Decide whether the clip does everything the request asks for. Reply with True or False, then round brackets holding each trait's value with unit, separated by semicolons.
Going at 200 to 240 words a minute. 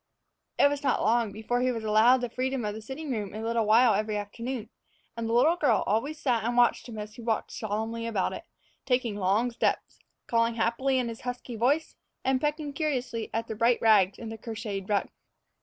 True (205 wpm)